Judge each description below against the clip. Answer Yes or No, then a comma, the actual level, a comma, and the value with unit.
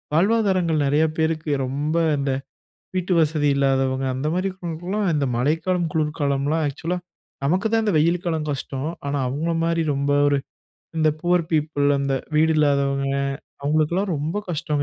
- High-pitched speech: No, medium, 155 Hz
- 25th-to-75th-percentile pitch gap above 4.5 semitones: No, average, 3.4 semitones